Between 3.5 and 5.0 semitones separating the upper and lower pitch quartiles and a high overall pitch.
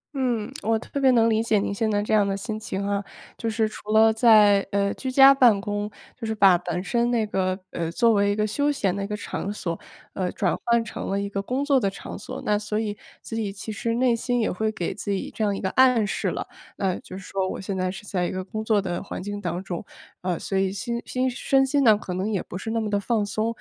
No: narrow, 2.6 semitones; high, 210 Hz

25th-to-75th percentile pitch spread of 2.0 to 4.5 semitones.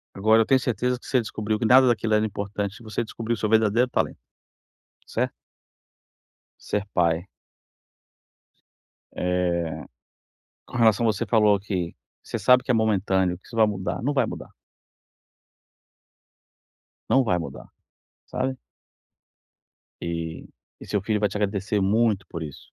Yes: average, 3.2 semitones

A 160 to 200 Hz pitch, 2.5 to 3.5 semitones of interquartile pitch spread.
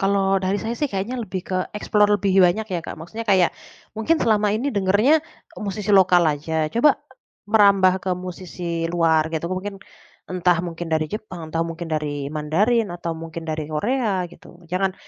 No: medium, 185 Hz; average, 3.9 semitones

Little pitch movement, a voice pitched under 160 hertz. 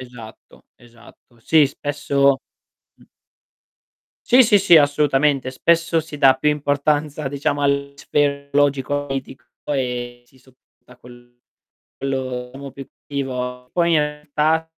Yes: narrow, 2.3 semitones; medium, 140 Hz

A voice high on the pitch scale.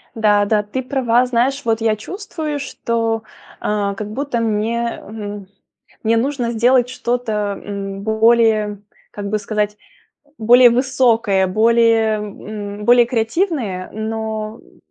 Yes: high, 225 Hz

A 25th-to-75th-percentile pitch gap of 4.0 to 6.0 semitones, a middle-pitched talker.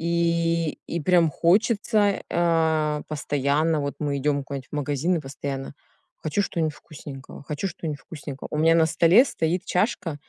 No: average, 2.7 semitones; medium, 160 Hz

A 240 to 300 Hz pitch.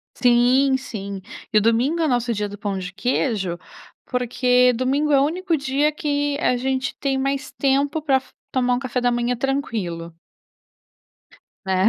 Yes: very high, 250 Hz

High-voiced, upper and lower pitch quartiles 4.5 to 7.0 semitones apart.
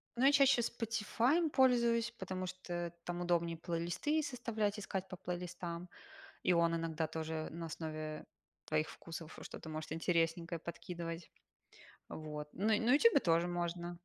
No: medium, 175 Hz; average, 5.1 semitones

